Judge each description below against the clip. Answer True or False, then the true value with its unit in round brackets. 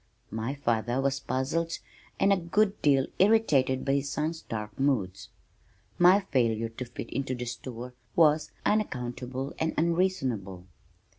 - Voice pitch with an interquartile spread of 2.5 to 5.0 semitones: False (5.5 semitones)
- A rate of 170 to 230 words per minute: False (135 wpm)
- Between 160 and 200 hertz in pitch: False (135 Hz)